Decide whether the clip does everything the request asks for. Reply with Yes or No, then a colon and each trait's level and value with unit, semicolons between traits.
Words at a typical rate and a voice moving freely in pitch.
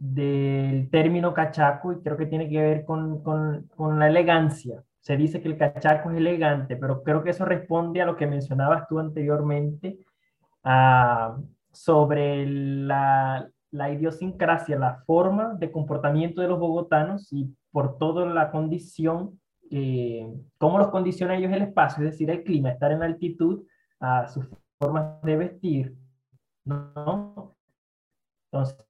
No: average, 145 wpm; average, 3.1 semitones